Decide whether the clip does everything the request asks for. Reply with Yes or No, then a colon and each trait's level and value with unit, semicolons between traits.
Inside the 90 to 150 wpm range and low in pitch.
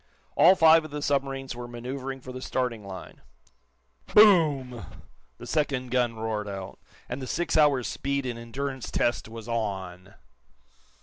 Yes: average, 145 wpm; low, 130 Hz